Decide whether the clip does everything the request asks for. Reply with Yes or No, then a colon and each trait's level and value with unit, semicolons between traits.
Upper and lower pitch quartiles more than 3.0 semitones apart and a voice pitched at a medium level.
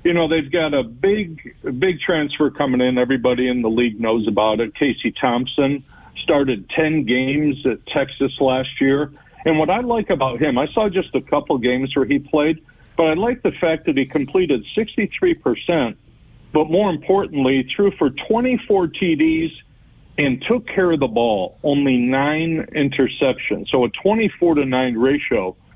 Yes: average, 4.7 semitones; medium, 145 Hz